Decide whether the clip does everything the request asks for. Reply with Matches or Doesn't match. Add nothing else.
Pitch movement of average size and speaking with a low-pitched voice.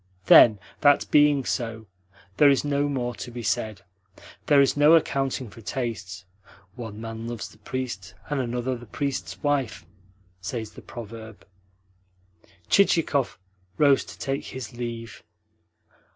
Matches